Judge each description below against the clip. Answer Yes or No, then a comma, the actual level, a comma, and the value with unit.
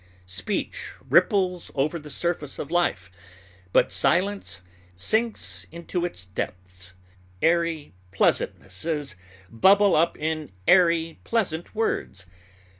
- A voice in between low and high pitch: Yes, medium, 160 Hz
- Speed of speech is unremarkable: No, slow, 100 wpm